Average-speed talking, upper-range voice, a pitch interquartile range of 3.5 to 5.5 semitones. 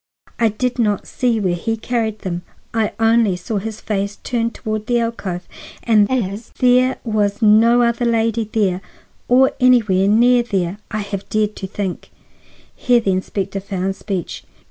No: average, 160 wpm; high, 215 Hz; average, 3.0 semitones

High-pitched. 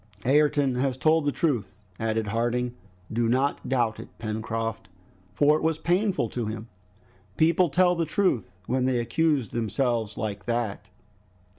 No: low, 125 Hz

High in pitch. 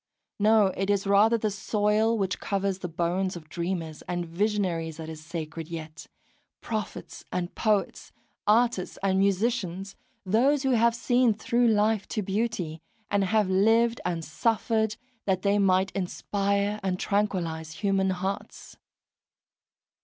Yes: high, 195 Hz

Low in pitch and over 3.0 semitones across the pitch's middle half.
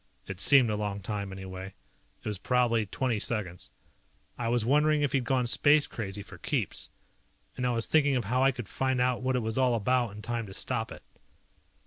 Yes: low, 120 Hz; average, 3.7 semitones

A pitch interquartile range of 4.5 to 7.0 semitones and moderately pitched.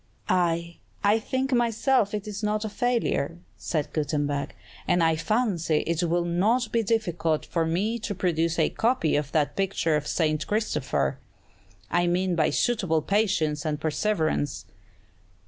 Yes: average, 5.1 semitones; medium, 175 Hz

